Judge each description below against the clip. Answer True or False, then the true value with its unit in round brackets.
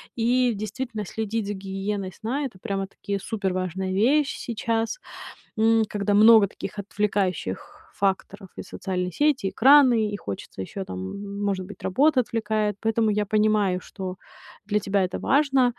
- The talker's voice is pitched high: True (210 Hz)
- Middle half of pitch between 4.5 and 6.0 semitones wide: False (2.8 semitones)